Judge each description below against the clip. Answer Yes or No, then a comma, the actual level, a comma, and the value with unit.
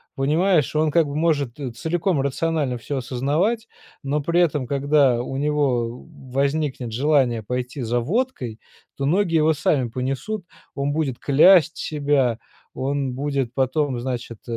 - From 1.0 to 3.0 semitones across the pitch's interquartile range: No, average, 3.5 semitones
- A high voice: No, medium, 140 Hz